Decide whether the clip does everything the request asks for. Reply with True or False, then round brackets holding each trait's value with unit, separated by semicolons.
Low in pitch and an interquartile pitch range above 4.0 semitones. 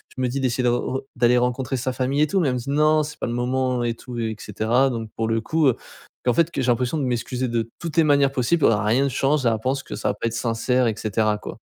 False (125 Hz; 2.8 semitones)